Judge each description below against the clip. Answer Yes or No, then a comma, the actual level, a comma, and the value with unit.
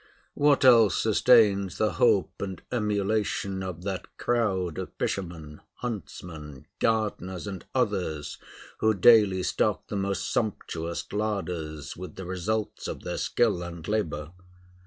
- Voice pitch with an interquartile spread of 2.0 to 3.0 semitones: No, average, 3.8 semitones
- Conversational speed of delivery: No, slow, 125 wpm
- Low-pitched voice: Yes, very low, 95 Hz